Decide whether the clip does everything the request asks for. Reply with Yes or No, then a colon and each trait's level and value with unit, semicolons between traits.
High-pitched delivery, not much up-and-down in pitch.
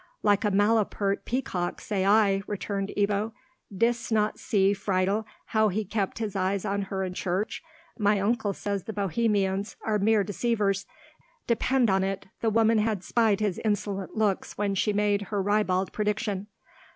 Yes: high, 205 Hz; narrow, 1.8 semitones